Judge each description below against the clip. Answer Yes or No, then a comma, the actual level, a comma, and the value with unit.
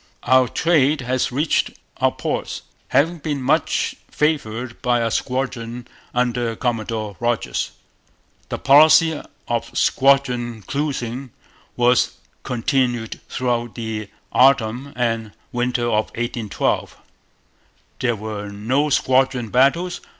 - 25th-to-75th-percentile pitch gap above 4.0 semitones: No, average, 2.8 semitones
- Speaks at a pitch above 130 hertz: No, low, 125 Hz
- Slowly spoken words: Yes, slow, 105 wpm